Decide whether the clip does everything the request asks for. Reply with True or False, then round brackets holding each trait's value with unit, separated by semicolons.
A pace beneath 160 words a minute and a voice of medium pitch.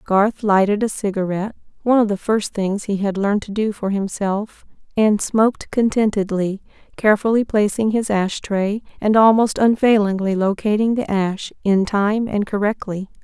False (145 wpm; 205 Hz)